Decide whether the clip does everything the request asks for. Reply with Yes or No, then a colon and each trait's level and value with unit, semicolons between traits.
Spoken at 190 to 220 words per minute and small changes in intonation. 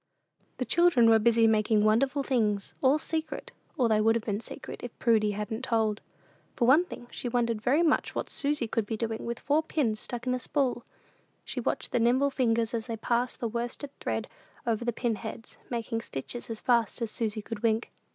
Yes: average, 200 wpm; narrow, 2.3 semitones